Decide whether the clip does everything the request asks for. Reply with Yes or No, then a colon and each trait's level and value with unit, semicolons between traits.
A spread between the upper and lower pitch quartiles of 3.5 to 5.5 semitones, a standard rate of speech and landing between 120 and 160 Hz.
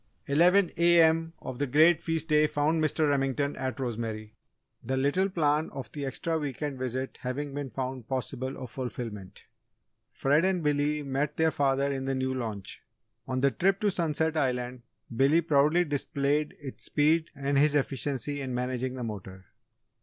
No: average, 3.0 semitones; average, 165 wpm; medium, 140 Hz